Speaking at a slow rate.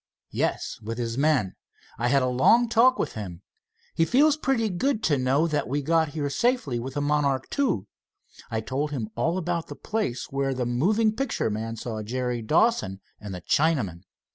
No: average, 185 wpm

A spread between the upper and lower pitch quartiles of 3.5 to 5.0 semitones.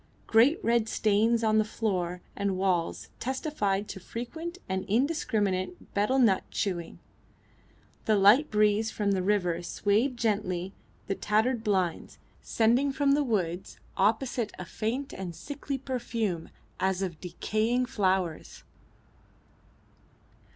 Yes: average, 4.1 semitones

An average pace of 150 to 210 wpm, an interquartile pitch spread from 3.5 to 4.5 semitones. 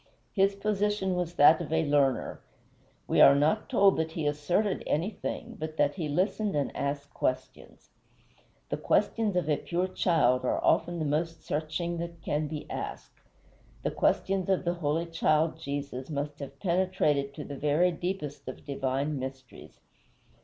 Yes: average, 160 wpm; average, 3.9 semitones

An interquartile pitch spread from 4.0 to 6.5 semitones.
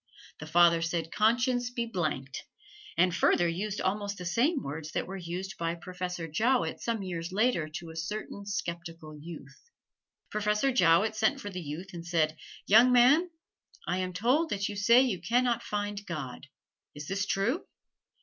Yes: average, 4.8 semitones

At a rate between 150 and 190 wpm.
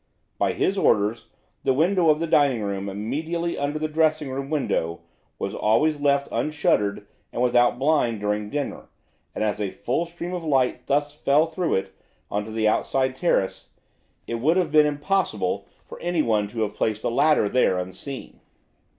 Yes: average, 170 wpm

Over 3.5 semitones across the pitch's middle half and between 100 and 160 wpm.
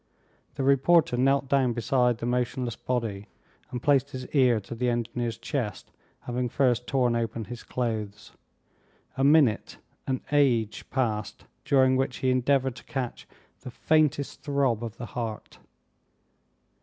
No: narrow, 2.5 semitones; average, 140 wpm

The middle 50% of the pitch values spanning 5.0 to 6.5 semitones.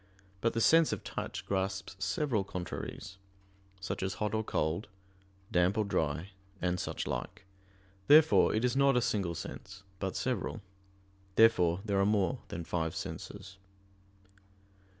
No: average, 3.4 semitones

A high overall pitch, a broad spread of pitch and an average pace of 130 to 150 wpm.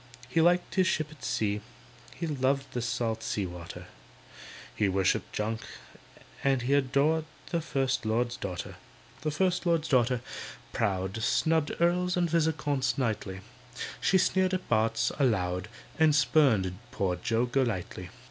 No: low, 130 Hz; wide, 6.5 semitones; average, 140 wpm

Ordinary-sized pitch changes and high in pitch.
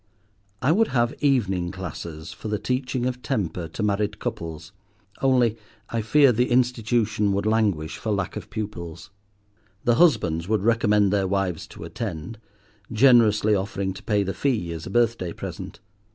No: average, 4.1 semitones; low, 105 Hz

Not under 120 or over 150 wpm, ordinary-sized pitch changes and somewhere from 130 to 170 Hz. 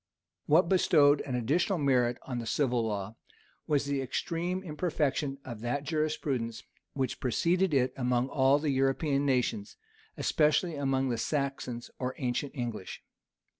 Yes: slow, 135 wpm; average, 3.5 semitones; low, 135 Hz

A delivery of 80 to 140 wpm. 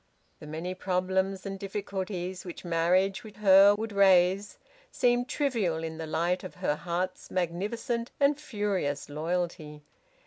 Yes: slow, 135 wpm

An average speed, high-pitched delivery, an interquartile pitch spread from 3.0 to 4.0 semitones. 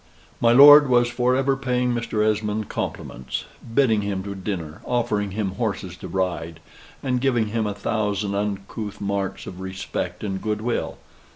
No: average, 160 wpm; low, 105 Hz; average, 3.6 semitones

